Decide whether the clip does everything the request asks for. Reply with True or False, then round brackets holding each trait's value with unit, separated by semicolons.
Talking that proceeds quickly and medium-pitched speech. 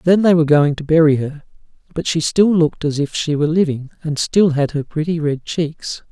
True (225 wpm; 155 Hz)